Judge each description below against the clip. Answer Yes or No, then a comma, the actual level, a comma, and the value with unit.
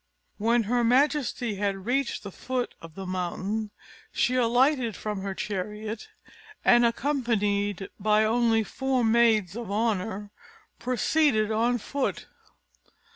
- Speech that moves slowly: Yes, slow, 120 wpm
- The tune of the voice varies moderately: Yes, average, 3.1 semitones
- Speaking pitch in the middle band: No, high, 225 Hz